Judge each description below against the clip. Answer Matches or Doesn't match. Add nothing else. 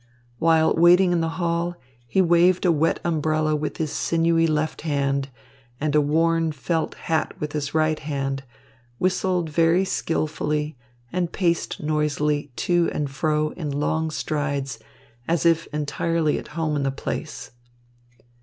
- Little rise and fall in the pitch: Matches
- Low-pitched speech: Doesn't match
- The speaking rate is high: Doesn't match